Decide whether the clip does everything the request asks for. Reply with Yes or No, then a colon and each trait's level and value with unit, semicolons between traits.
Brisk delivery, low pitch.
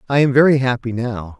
Yes: fast, 215 wpm; low, 125 Hz